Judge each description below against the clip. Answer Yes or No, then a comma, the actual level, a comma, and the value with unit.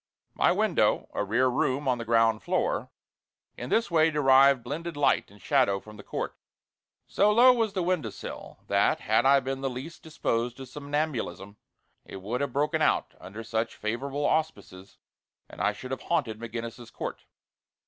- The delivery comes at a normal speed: Yes, average, 170 wpm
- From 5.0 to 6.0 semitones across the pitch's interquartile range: No, average, 4.6 semitones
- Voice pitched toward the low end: Yes, low, 130 Hz